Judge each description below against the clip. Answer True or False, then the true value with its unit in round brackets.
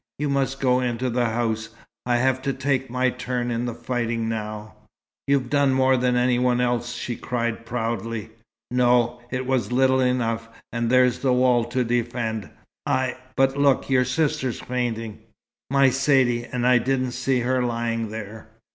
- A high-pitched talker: False (125 Hz)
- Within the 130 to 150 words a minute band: False (170 wpm)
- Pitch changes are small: True (1.9 semitones)